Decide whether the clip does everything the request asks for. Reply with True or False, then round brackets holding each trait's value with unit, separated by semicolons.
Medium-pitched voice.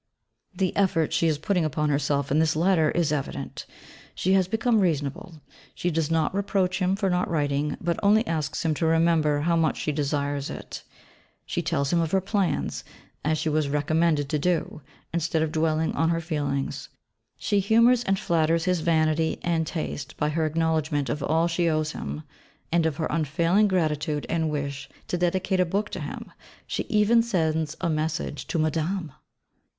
True (160 Hz)